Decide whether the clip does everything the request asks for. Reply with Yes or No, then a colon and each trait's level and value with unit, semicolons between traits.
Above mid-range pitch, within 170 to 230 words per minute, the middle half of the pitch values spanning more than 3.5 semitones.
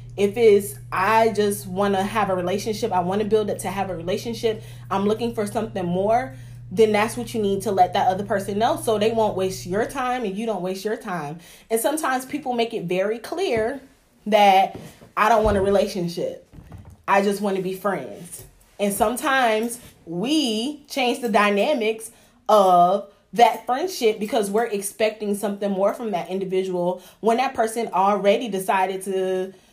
No: high, 210 Hz; average, 180 wpm; average, 3.1 semitones